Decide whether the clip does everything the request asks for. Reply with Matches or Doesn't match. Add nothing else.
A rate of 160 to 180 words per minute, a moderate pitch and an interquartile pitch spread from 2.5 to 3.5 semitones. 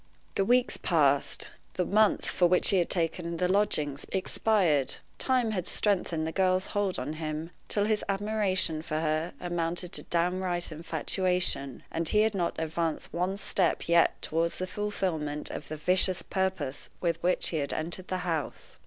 Matches